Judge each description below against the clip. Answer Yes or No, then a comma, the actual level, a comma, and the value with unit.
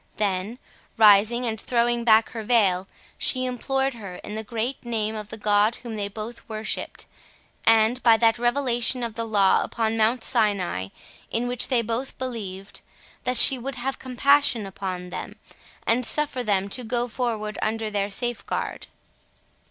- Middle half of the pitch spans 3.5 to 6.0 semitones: No, narrow, 2.6 semitones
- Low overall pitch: No, high, 225 Hz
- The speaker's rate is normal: Yes, average, 160 wpm